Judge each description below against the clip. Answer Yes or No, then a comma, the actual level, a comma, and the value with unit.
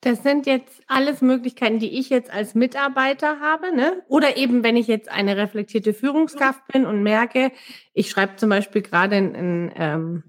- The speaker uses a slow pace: No, average, 180 wpm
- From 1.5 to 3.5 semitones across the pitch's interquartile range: No, average, 4.5 semitones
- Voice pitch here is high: Yes, high, 245 Hz